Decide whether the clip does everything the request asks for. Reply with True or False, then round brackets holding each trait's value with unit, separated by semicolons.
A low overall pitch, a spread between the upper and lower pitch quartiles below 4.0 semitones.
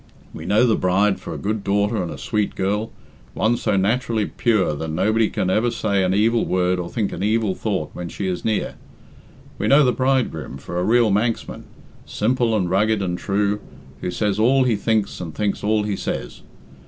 True (105 Hz; 3.0 semitones)